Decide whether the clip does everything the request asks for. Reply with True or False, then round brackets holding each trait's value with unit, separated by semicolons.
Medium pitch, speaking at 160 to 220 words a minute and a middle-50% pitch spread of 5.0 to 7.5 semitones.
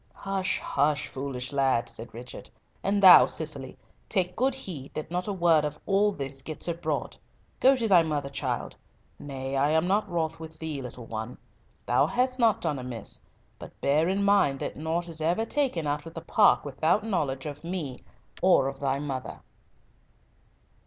True (155 Hz; 175 wpm; 5.3 semitones)